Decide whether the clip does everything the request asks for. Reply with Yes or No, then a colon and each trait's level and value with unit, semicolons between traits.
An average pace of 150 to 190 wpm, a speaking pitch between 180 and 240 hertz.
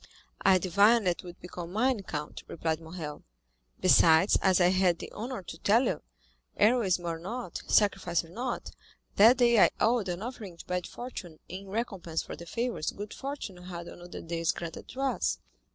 Yes: average, 185 wpm; medium, 185 Hz